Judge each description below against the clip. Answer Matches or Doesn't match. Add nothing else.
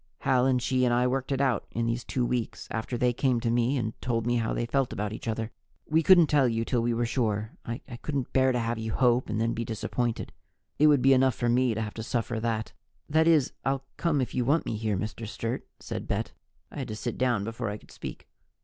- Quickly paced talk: Matches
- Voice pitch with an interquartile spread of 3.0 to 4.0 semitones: Doesn't match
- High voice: Doesn't match